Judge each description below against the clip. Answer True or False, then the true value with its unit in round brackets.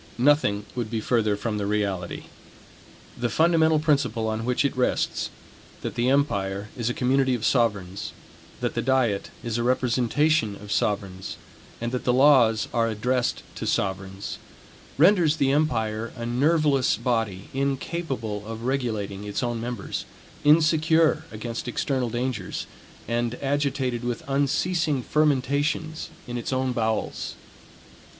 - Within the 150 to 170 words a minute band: False (135 wpm)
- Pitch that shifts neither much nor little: True (4.2 semitones)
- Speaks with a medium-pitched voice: False (125 Hz)